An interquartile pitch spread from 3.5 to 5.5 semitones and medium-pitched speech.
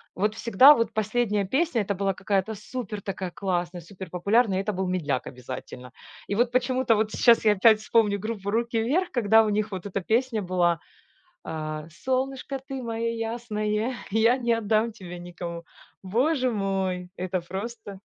No: average, 3.8 semitones; high, 210 Hz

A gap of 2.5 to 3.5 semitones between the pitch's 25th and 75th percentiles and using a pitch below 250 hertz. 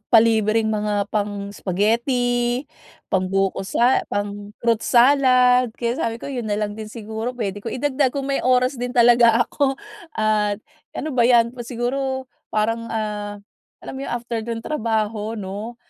Yes: average, 2.9 semitones; high, 230 Hz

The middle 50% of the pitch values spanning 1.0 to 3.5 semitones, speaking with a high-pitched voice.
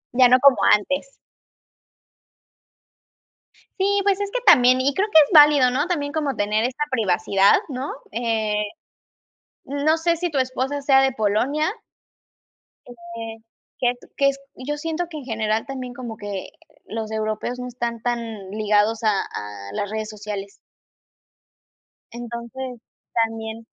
No: average, 4.3 semitones; high, 245 Hz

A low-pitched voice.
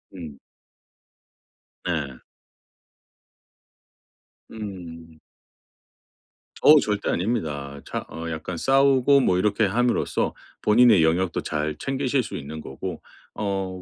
Yes: very low, 95 Hz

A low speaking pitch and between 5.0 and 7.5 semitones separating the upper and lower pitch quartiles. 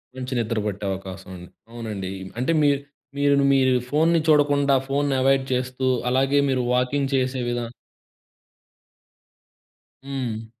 No: low, 130 Hz; average, 3.0 semitones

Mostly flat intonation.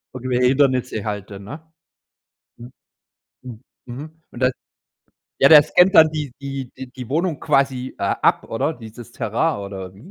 No: average, 4.3 semitones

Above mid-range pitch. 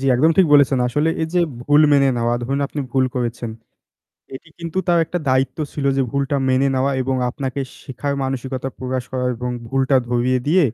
No: low, 135 Hz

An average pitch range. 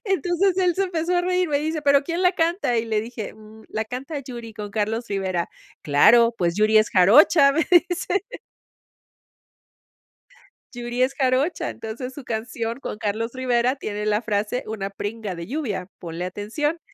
No: wide, 6.2 semitones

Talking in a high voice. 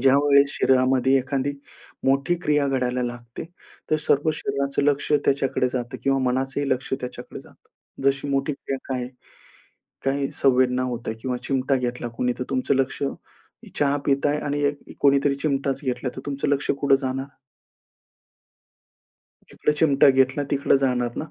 No: low, 135 Hz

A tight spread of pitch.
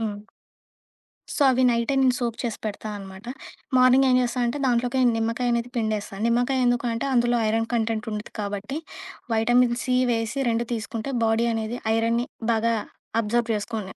Yes: narrow, 1.8 semitones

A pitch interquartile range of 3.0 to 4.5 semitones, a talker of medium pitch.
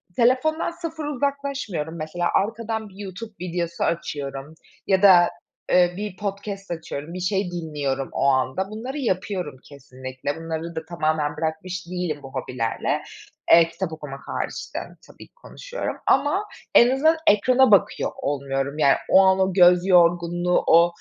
No: average, 5.1 semitones; medium, 175 Hz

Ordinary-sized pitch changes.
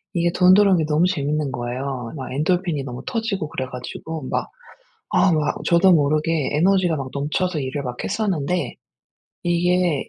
Yes: average, 4.5 semitones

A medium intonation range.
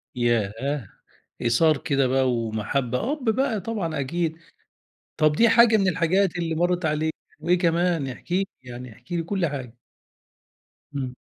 No: wide, 5.9 semitones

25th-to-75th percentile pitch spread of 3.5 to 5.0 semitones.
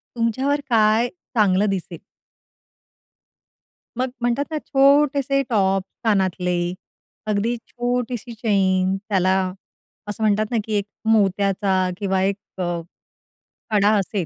Yes: average, 4.0 semitones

